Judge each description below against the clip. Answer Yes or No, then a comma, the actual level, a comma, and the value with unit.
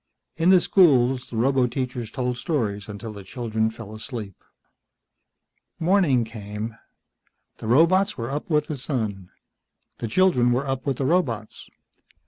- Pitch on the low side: Yes, low, 125 Hz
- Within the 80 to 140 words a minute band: Yes, slow, 135 wpm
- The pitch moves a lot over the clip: No, average, 4.9 semitones